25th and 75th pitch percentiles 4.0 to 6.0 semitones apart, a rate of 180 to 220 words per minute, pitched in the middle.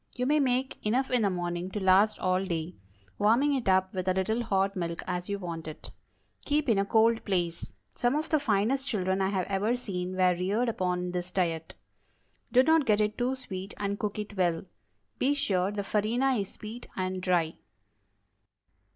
No: average, 4.4 semitones; average, 190 wpm; high, 200 Hz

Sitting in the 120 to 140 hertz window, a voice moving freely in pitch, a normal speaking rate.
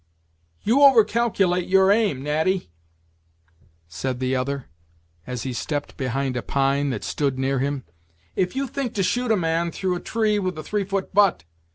No: medium, 170 Hz; wide, 7.0 semitones; average, 175 wpm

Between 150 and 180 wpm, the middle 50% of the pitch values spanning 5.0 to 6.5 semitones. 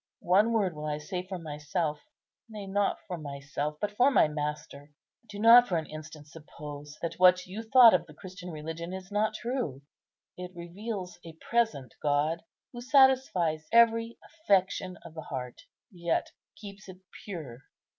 Yes: average, 160 wpm; wide, 5.4 semitones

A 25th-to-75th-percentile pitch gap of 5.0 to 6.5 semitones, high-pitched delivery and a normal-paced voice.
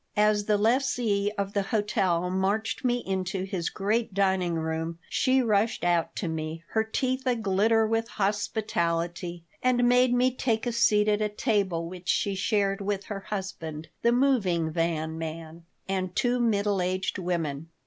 No: average, 4.3 semitones; high, 200 Hz; average, 160 wpm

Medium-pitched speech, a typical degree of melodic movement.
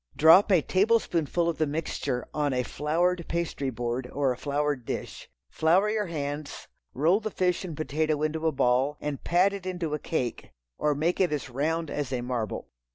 Yes: medium, 155 Hz; average, 3.5 semitones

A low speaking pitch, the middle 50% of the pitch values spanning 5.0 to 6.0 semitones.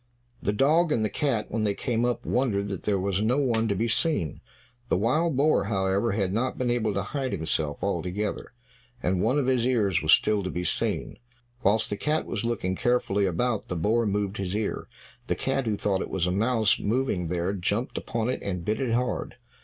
No: low, 110 Hz; average, 4.2 semitones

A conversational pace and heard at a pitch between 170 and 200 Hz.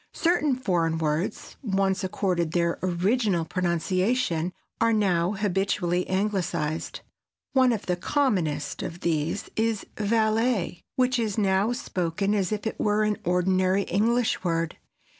No: slow, 125 wpm; high, 190 Hz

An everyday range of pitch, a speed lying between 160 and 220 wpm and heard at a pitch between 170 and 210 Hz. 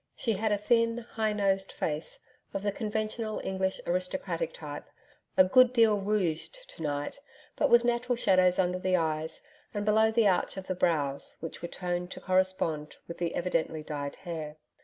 Yes: average, 4.4 semitones; average, 175 wpm; high, 190 Hz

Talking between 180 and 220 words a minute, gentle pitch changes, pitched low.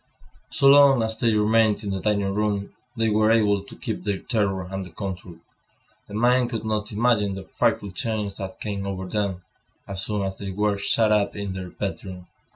Yes: average, 190 wpm; narrow, 2.1 semitones; low, 105 Hz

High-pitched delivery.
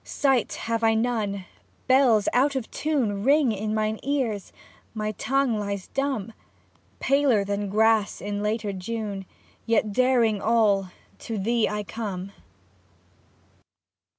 Yes: high, 220 Hz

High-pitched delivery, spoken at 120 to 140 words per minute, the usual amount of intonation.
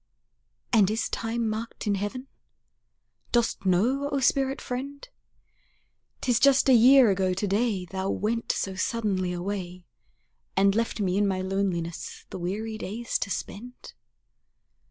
Yes: high, 210 Hz; slow, 135 wpm; average, 4.0 semitones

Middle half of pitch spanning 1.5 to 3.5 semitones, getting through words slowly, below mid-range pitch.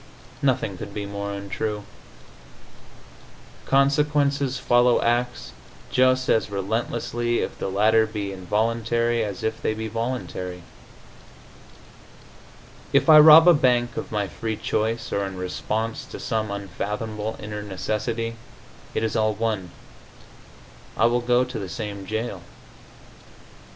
Yes: average, 2.8 semitones; slow, 125 wpm; low, 110 Hz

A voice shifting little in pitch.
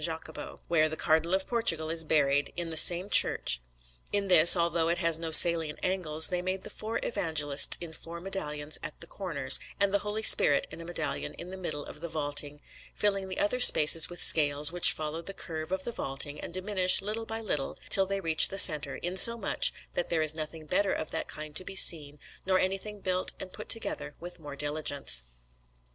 No: average, 3.7 semitones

